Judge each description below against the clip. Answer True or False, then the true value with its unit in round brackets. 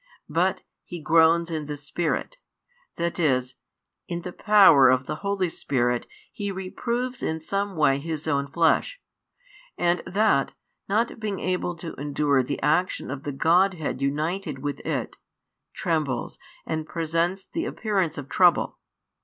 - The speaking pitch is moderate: True (165 Hz)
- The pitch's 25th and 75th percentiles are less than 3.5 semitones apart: False (4.5 semitones)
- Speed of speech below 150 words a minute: True (140 wpm)